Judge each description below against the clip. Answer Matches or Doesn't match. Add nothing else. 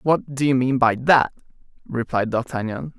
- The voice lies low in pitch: Matches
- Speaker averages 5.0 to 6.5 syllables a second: Doesn't match